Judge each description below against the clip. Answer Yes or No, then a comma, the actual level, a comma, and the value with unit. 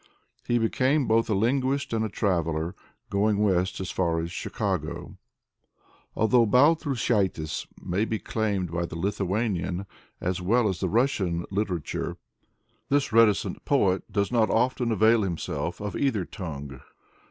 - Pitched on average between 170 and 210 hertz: No, low, 105 Hz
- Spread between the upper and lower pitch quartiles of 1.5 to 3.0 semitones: No, average, 4.3 semitones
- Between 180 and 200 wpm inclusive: No, slow, 135 wpm